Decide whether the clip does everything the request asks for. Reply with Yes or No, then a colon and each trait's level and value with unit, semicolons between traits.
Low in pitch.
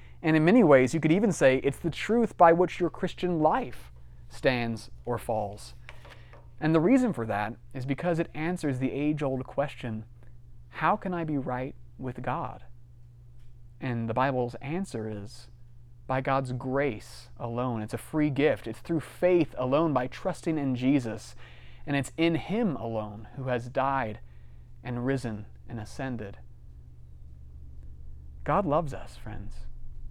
Yes: low, 125 Hz